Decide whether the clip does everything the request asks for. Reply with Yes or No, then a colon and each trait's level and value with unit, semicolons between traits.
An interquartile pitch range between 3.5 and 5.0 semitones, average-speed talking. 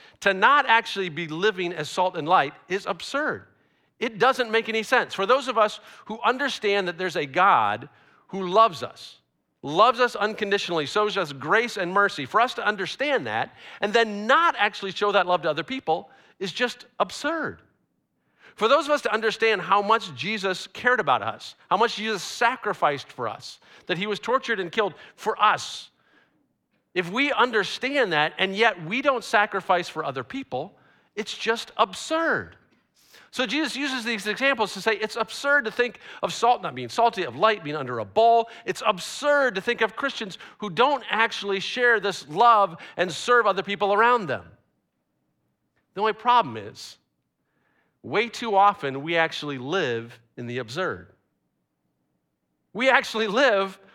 Yes: average, 3.9 semitones; average, 170 wpm